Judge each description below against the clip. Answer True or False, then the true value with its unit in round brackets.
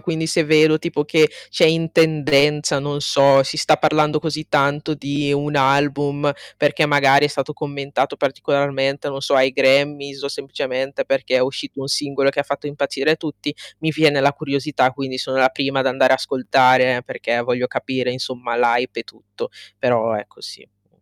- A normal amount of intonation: False (2.0 semitones)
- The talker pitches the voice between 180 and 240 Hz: False (140 Hz)